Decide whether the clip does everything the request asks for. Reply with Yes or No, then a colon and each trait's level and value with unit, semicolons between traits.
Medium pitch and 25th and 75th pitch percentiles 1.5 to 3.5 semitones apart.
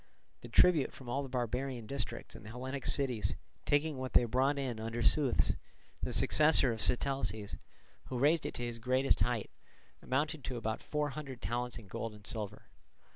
No: low, 125 Hz; average, 3.1 semitones